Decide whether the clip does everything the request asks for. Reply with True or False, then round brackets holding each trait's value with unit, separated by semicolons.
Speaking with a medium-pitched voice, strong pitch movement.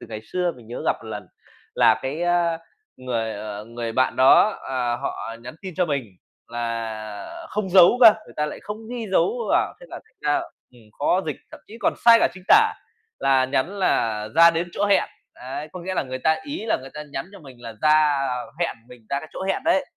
True (150 Hz; 7.9 semitones)